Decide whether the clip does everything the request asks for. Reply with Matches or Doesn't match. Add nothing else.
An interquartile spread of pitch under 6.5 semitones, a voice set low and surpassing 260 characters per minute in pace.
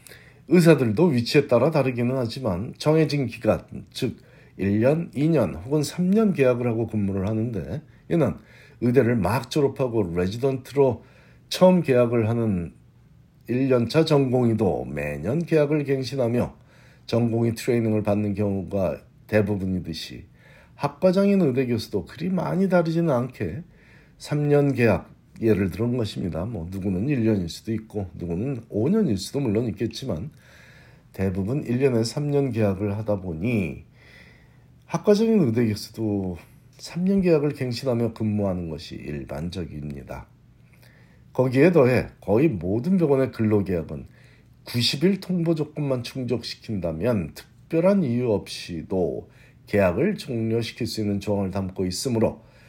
Matches